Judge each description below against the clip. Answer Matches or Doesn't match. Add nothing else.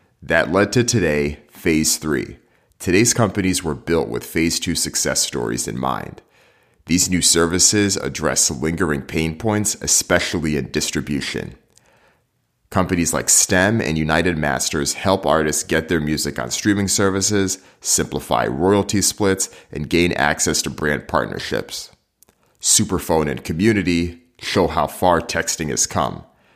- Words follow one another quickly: Doesn't match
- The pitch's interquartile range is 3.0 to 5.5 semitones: Matches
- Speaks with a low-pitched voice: Matches